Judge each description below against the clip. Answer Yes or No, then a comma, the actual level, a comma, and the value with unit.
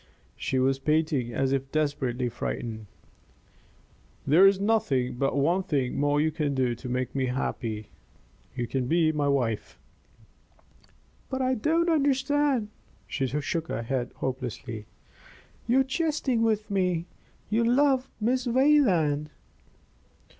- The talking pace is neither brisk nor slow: No, slow, 125 wpm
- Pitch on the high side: No, medium, 150 Hz